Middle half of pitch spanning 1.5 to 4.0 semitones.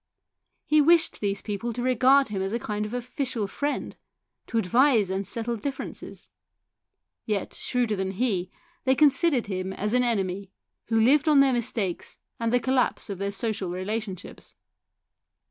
No: average, 4.4 semitones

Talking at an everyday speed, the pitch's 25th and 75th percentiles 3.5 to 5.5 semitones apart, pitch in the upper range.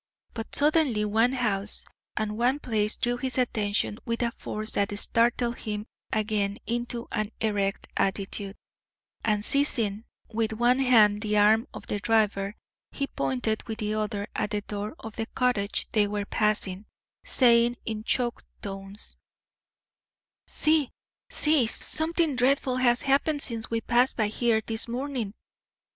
No: average, 145 wpm; average, 2.8 semitones; high, 225 Hz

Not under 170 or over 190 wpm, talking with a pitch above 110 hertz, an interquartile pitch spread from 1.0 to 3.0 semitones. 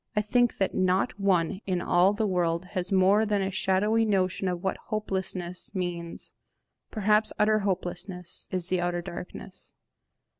No: average, 150 wpm; high, 190 Hz; narrow, 2.6 semitones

